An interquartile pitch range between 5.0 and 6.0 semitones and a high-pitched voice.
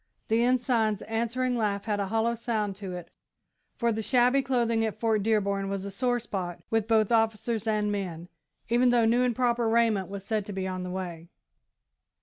No: average, 2.9 semitones; high, 220 Hz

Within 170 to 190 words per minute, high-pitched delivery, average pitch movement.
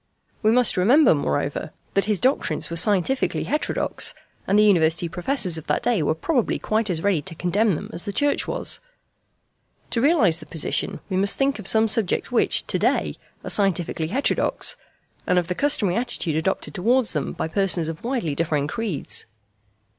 No: average, 175 wpm; high, 195 Hz; wide, 5.7 semitones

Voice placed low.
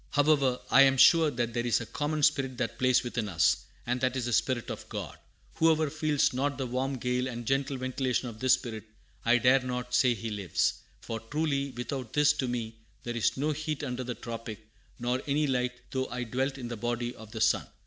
Yes: low, 125 Hz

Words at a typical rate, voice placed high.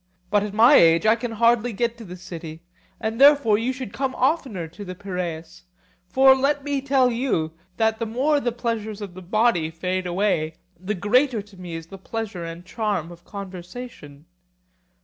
Yes: average, 185 wpm; high, 210 Hz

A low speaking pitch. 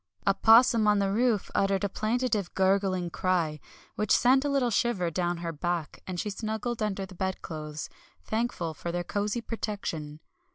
No: high, 195 Hz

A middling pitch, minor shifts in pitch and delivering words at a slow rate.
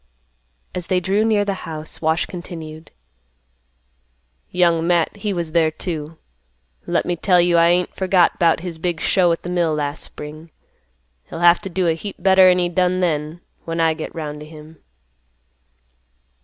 No: medium, 170 Hz; narrow, 2.2 semitones; average, 170 wpm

